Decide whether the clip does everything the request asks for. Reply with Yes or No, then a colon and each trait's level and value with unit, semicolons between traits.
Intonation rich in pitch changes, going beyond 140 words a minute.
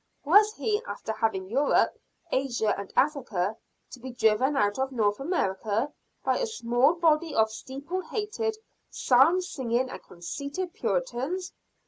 No: wide, 8.0 semitones; slow, 135 wpm